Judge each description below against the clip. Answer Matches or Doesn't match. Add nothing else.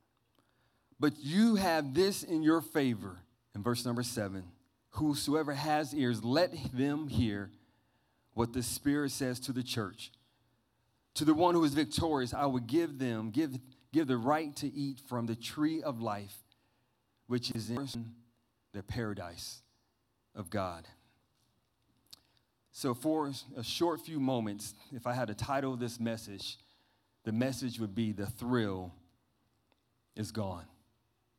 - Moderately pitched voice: Doesn't match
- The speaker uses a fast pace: Doesn't match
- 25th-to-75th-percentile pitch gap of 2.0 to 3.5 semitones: Doesn't match